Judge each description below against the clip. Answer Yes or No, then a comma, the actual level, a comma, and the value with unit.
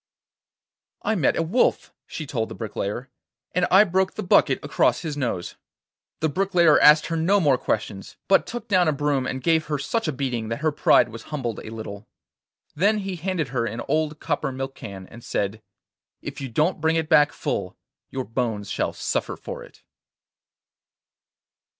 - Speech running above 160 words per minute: Yes, average, 180 wpm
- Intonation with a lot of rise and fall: Yes, wide, 5.8 semitones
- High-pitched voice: No, medium, 145 Hz